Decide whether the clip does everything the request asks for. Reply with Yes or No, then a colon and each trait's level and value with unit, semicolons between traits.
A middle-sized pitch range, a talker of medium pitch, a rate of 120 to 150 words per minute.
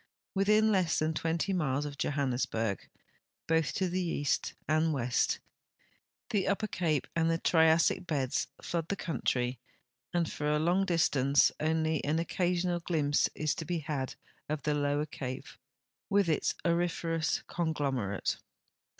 Yes: average, 3.2 semitones; medium, 160 Hz; average, 140 wpm